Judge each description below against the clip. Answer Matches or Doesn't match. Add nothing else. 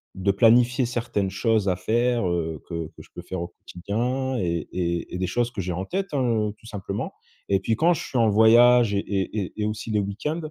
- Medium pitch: Doesn't match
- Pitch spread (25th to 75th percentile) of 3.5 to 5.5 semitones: Matches